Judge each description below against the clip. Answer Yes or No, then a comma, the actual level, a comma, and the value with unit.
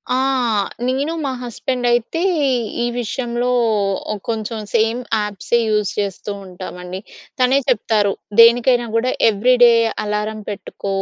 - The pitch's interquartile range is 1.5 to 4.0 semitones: Yes, average, 2.9 semitones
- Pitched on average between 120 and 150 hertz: No, high, 230 Hz